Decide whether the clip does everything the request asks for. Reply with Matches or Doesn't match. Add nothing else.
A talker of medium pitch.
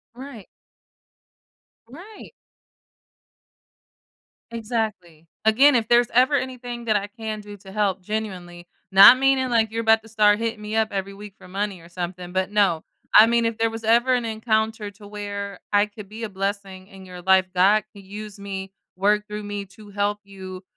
Doesn't match